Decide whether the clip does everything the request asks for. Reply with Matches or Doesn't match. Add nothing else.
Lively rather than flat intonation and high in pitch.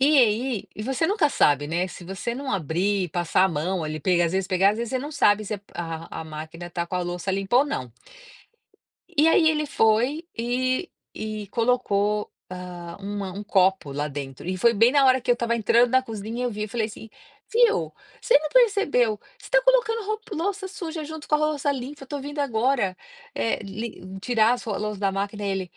Matches